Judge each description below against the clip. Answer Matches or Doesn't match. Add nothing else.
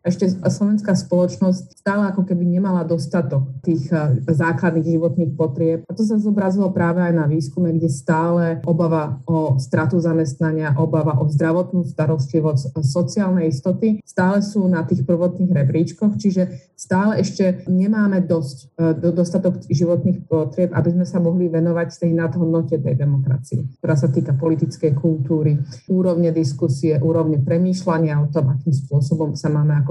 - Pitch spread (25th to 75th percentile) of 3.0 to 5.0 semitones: Doesn't match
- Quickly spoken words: Doesn't match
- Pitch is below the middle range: Doesn't match